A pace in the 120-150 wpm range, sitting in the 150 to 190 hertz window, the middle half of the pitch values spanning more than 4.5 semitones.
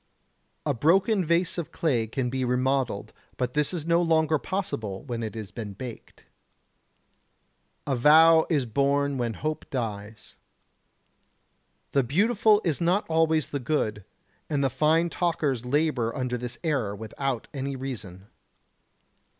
No: slow, 135 wpm; medium, 140 Hz; average, 5.1 semitones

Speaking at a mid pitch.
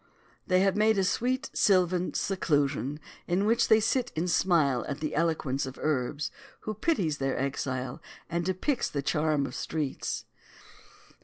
Yes: medium, 165 Hz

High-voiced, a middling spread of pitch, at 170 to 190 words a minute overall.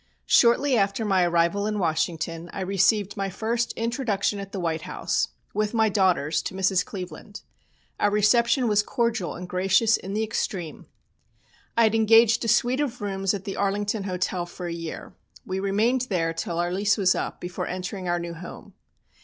Yes: high, 195 Hz; average, 3.4 semitones; average, 180 wpm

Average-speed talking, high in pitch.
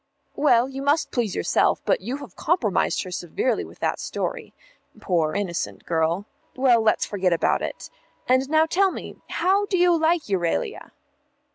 Yes: average, 160 wpm; very high, 255 Hz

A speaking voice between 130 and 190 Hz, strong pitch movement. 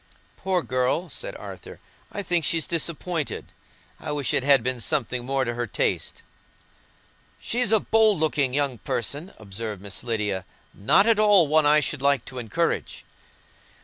Yes: medium, 140 Hz; wide, 6.1 semitones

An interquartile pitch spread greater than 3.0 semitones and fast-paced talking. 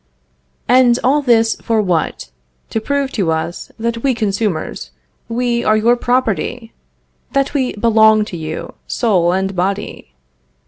No: average, 4.1 semitones; slow, 135 wpm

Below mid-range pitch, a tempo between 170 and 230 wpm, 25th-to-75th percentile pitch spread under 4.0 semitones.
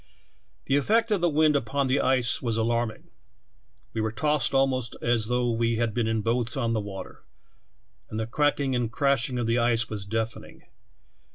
Yes: low, 120 Hz; average, 190 wpm; average, 3.3 semitones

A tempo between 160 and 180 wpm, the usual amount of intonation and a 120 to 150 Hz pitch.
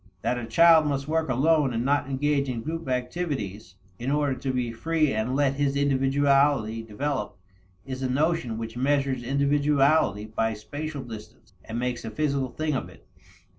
Yes: average, 170 wpm; average, 3.5 semitones; low, 135 Hz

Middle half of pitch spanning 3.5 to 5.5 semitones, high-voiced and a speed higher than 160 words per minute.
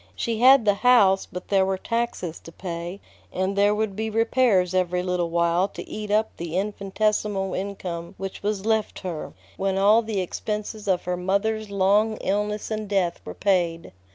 No: average, 2.8 semitones; high, 195 Hz; average, 175 wpm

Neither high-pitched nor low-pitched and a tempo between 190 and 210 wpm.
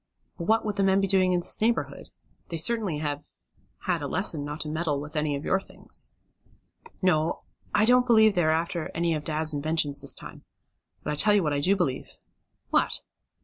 Yes: medium, 170 Hz; fast, 205 wpm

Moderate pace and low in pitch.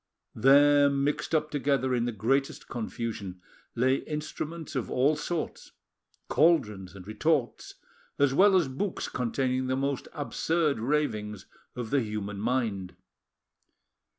No: slow, 125 wpm; low, 130 Hz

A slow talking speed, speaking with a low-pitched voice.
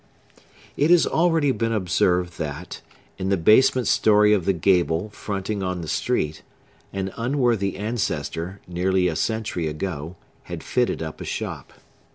No: average, 145 wpm; very low, 95 Hz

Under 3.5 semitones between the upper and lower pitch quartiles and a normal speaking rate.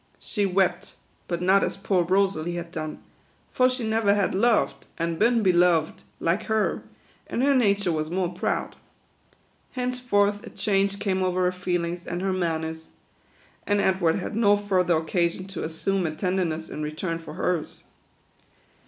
Yes: average, 3.1 semitones; average, 160 wpm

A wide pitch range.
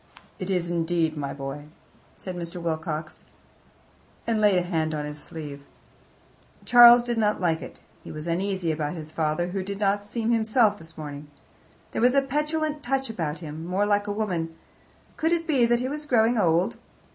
Yes: wide, 6.3 semitones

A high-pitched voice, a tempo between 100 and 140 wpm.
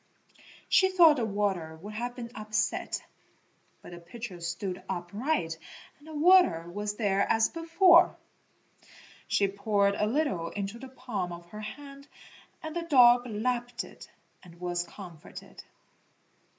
Yes: high, 215 Hz; slow, 135 wpm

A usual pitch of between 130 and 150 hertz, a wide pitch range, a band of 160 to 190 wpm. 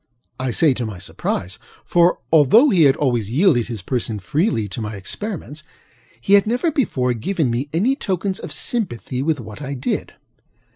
Yes: medium, 140 Hz; wide, 8.2 semitones; average, 175 wpm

